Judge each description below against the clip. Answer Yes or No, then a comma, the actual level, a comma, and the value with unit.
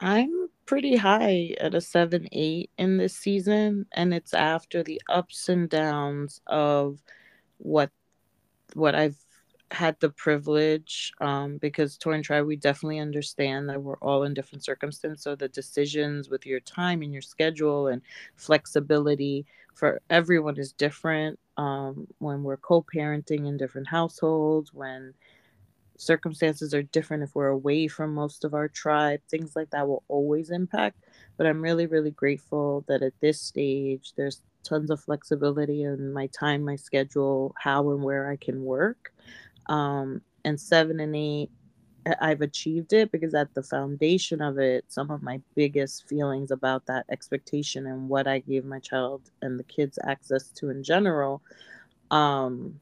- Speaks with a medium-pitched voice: Yes, medium, 150 Hz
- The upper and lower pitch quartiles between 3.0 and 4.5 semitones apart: No, narrow, 2.5 semitones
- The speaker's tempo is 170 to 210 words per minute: No, average, 160 wpm